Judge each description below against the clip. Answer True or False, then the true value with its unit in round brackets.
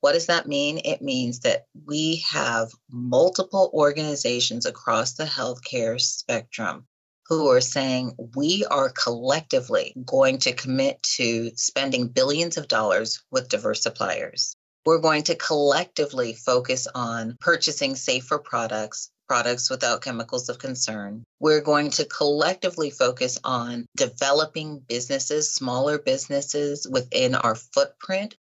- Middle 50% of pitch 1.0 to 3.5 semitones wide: False (4.4 semitones)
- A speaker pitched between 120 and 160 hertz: True (140 Hz)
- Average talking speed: False (125 wpm)